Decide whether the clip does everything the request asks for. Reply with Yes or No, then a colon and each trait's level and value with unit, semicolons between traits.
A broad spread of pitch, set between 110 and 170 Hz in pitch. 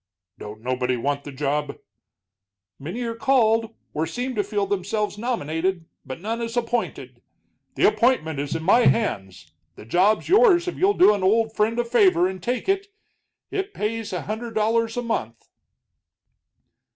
No: wide, 6.8 semitones; high, 215 Hz